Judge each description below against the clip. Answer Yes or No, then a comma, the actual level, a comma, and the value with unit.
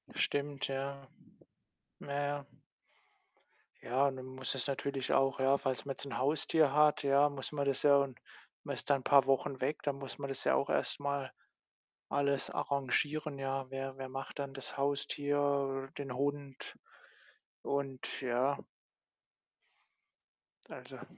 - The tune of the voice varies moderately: No, narrow, 1.0 semitones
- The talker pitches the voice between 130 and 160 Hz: Yes, medium, 140 Hz